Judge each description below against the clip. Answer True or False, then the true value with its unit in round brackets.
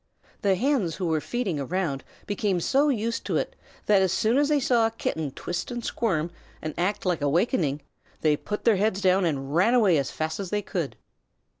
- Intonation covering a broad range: True (5.8 semitones)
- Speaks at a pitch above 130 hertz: True (190 Hz)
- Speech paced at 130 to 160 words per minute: False (200 wpm)